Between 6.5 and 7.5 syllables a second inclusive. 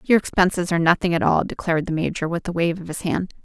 Yes: 6.8 syllables/s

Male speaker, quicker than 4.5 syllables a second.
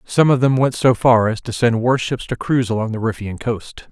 Yes: male; 5.3 syllables/s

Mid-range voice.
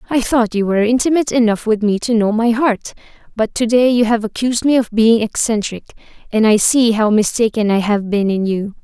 No: high, 225 Hz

